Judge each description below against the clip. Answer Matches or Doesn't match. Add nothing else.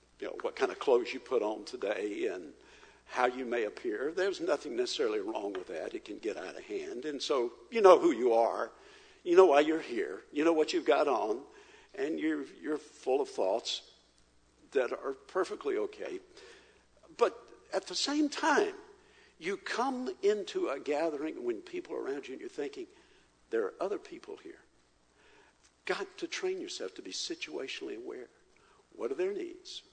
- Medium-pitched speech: Doesn't match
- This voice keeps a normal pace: Matches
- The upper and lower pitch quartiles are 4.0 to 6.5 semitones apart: Doesn't match